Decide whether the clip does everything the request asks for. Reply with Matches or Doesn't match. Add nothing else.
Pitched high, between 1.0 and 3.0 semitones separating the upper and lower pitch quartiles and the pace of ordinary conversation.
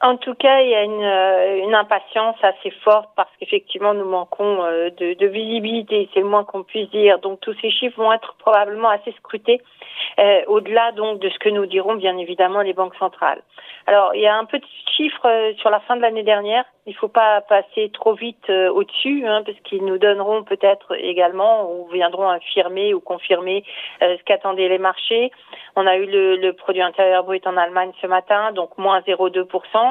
Matches